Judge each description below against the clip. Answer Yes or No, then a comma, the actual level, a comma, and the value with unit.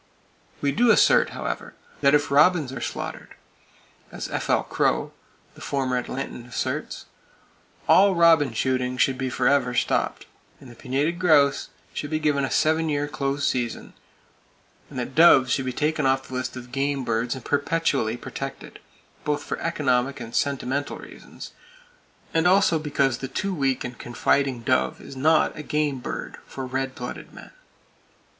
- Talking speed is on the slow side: No, average, 155 wpm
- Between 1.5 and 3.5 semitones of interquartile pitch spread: Yes, average, 2.8 semitones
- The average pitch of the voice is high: No, low, 135 Hz